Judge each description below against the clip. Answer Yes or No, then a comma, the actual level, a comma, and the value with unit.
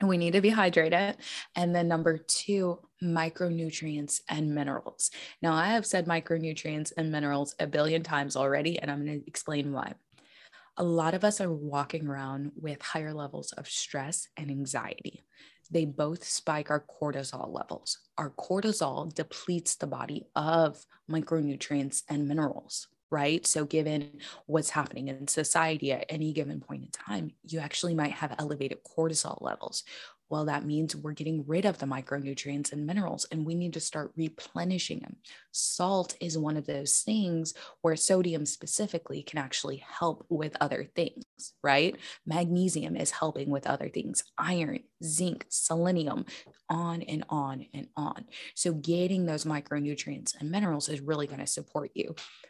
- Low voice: No, medium, 160 Hz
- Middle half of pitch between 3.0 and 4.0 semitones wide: No, narrow, 2.6 semitones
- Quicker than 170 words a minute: No, average, 160 wpm